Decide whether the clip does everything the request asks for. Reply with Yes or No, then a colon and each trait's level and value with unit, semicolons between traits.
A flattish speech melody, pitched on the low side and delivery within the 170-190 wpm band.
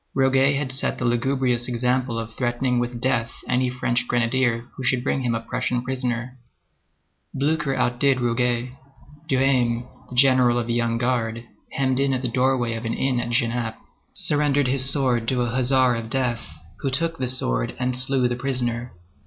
Yes: narrow, 1.6 semitones; low, 125 Hz; average, 175 wpm